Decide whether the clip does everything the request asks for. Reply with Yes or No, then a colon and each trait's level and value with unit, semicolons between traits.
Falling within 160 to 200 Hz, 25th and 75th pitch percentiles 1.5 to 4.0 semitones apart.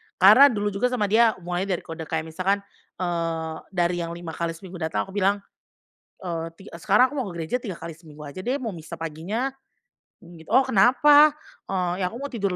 No: medium, 185 Hz; average, 4.9 semitones